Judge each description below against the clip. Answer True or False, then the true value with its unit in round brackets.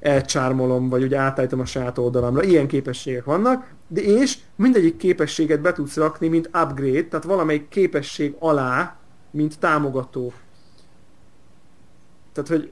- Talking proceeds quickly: False (125 wpm)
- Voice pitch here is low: False (150 Hz)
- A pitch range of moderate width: True (4.1 semitones)